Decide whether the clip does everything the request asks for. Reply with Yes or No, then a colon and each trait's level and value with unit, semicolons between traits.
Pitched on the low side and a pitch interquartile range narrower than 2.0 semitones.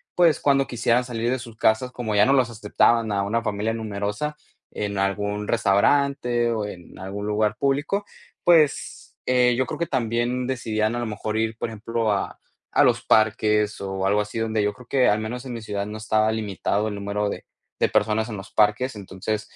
No: low, 110 Hz; average, 2.8 semitones